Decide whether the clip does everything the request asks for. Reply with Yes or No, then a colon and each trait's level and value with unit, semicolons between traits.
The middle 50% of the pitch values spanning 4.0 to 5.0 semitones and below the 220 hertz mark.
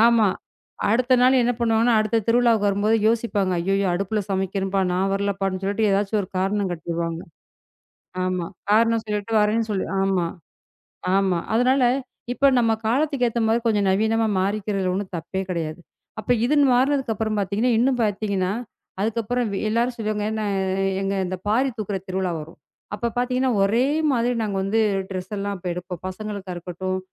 No: average, 3.2 semitones; high, 210 Hz